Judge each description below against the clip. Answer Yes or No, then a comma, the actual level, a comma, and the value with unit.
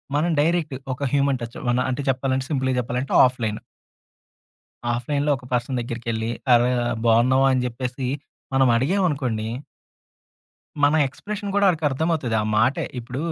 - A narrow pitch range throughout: No, average, 3.1 semitones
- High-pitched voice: No, low, 130 Hz